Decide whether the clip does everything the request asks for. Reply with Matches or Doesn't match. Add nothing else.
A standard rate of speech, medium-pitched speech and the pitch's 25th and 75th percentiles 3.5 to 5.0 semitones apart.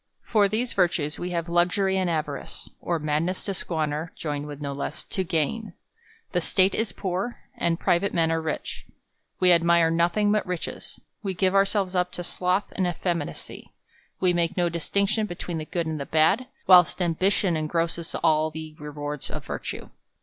Doesn't match